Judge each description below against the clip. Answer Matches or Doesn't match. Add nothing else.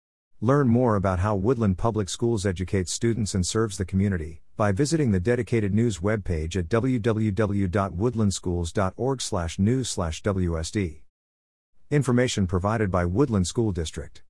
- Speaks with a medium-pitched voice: Doesn't match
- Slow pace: Matches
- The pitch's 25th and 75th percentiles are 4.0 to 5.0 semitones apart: Matches